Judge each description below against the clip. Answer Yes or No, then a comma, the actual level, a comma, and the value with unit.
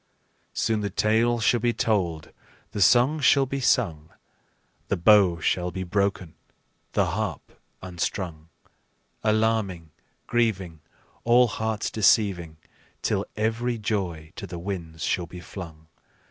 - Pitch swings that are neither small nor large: Yes, average, 4.6 semitones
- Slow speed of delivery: Yes, slow, 120 wpm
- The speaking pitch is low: Yes, low, 100 Hz